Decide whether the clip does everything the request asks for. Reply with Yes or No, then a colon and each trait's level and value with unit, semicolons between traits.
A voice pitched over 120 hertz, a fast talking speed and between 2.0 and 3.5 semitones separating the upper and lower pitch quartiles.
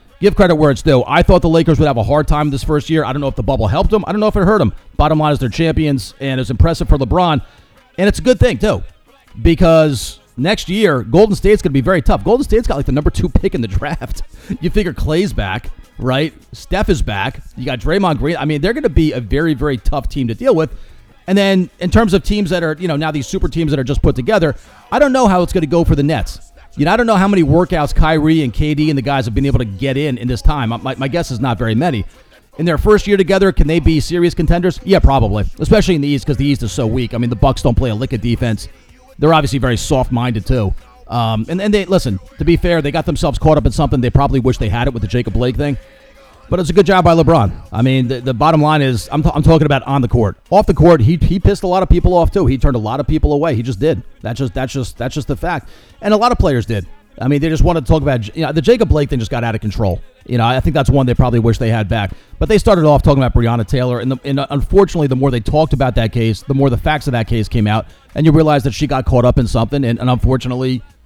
No: medium, 140 Hz; fast, 295 wpm; average, 5.3 semitones